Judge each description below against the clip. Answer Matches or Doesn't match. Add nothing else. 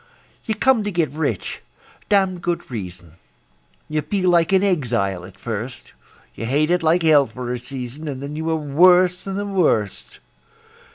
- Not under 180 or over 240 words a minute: Doesn't match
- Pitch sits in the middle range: Matches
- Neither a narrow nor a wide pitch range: Doesn't match